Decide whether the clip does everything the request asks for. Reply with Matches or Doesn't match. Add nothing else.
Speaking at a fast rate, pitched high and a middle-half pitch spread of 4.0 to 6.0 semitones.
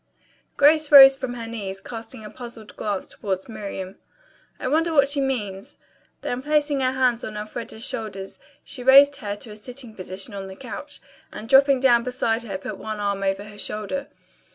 Doesn't match